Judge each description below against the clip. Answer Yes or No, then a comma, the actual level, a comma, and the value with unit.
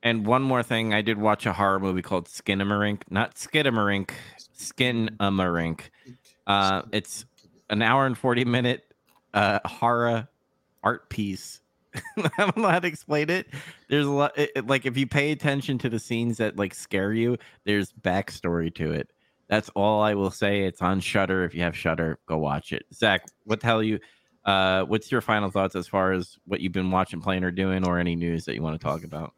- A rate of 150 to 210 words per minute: Yes, average, 200 wpm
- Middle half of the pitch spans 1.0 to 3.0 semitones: No, average, 4.7 semitones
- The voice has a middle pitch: No, low, 105 Hz